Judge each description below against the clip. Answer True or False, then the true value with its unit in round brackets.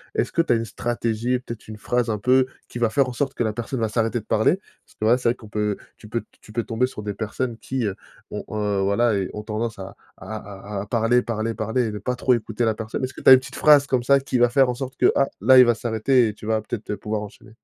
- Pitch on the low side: True (115 Hz)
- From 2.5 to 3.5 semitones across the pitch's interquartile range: True (2.8 semitones)